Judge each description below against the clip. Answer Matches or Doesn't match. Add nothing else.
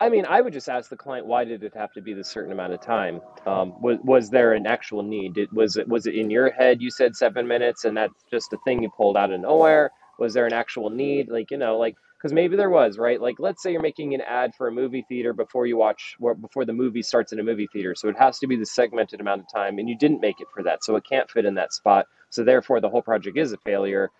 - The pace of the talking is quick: Matches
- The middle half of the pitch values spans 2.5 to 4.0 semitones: Matches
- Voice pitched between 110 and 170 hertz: Matches